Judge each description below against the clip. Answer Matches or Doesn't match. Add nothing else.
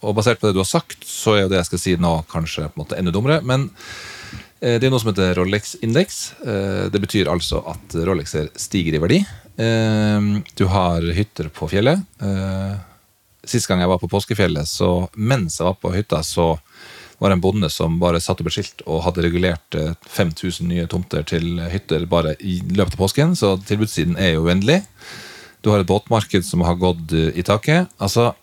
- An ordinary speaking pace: Matches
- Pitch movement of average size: Matches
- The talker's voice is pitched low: Matches